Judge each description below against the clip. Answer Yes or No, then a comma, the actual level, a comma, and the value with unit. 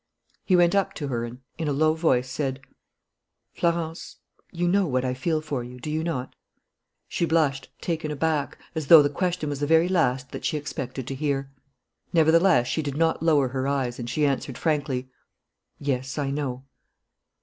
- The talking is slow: No, average, 180 wpm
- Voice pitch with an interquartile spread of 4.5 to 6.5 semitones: No, average, 3.6 semitones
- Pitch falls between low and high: Yes, medium, 145 Hz